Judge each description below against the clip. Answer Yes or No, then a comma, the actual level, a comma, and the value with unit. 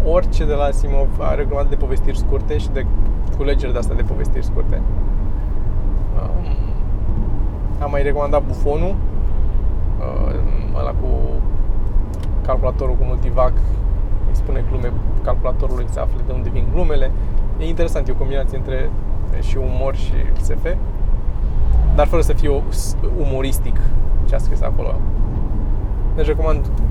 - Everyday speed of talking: Yes, average, 125 wpm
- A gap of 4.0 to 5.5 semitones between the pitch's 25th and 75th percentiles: No, average, 2.9 semitones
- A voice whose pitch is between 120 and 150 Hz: No, low, 100 Hz